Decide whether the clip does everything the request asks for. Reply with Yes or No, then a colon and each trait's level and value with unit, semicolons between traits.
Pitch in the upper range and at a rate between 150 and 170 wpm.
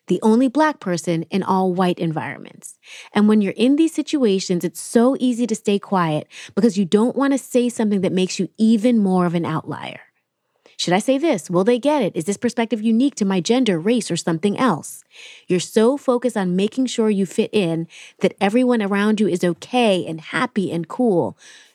No: high, 210 Hz; average, 200 wpm